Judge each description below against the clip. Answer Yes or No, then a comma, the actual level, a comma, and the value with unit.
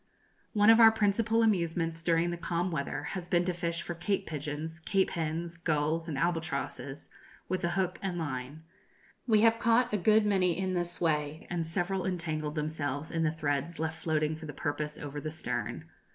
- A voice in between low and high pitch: Yes, medium, 170 Hz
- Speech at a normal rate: Yes, average, 185 wpm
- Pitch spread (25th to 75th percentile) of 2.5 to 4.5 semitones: Yes, average, 3.1 semitones